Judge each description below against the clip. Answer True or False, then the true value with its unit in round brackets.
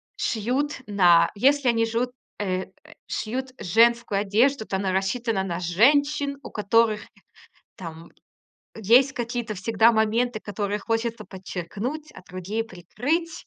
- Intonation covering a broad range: False (4.0 semitones)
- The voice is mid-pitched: False (225 Hz)